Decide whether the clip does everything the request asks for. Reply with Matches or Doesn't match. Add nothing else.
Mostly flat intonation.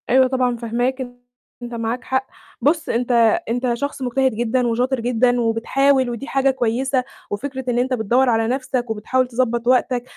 Matches